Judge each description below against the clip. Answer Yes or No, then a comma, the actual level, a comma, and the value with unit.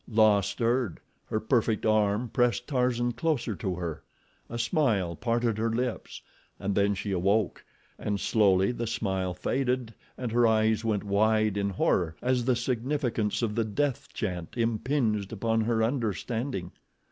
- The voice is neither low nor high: No, low, 110 Hz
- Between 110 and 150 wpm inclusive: Yes, average, 145 wpm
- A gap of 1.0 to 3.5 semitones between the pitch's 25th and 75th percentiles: Yes, average, 3.2 semitones